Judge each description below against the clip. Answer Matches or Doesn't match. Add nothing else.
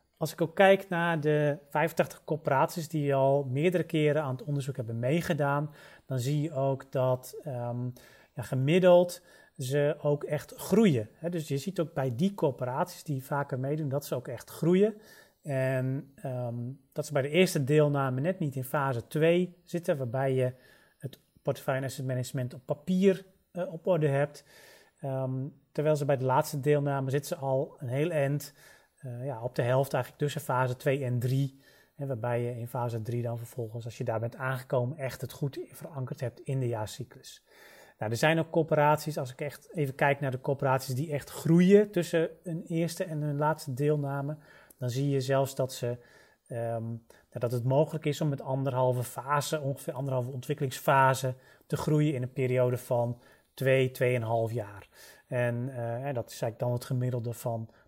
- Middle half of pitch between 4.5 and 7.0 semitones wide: Doesn't match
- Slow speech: Doesn't match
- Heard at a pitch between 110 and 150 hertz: Matches